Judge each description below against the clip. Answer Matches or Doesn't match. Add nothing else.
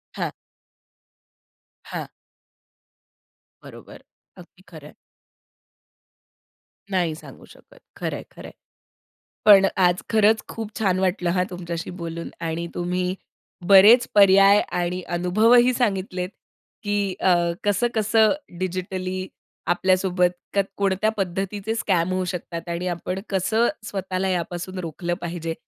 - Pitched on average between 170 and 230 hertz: Matches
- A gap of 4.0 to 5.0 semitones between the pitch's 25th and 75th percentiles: Doesn't match